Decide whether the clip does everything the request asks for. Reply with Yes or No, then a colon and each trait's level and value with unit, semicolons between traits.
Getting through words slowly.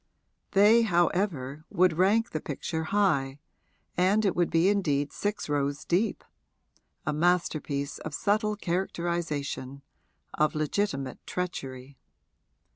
Yes: slow, 110 wpm